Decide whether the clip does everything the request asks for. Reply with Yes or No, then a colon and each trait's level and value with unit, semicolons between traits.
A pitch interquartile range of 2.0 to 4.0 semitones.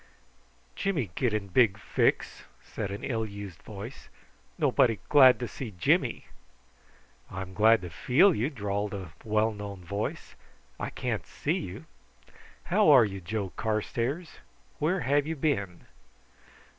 No: average, 5.1 semitones